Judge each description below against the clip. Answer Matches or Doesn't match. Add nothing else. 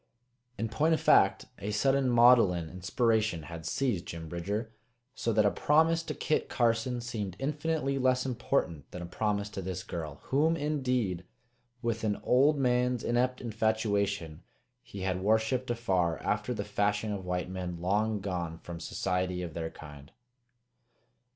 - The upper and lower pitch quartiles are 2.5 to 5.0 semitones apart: Doesn't match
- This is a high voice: Doesn't match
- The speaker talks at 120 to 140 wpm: Doesn't match